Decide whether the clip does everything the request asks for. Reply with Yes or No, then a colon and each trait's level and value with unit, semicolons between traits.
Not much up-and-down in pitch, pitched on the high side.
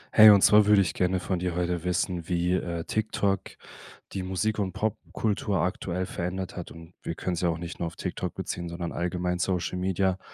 No: narrow, 1.8 semitones; very low, 90 Hz